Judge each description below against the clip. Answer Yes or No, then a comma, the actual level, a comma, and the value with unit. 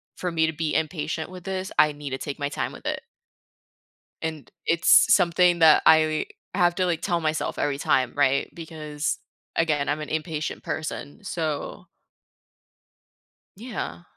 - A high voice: No, medium, 160 Hz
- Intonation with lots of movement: No, narrow, 2.6 semitones